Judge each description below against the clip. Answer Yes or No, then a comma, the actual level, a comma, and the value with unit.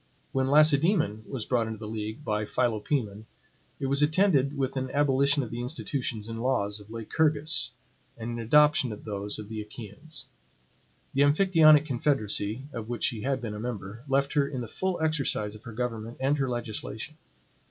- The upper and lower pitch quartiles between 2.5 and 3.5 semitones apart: No, average, 4.7 semitones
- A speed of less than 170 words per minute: No, average, 175 wpm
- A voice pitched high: No, low, 125 Hz